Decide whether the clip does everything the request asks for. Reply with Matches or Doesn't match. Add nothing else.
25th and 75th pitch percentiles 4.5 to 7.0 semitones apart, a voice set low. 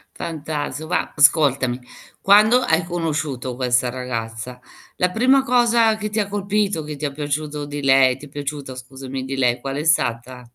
Doesn't match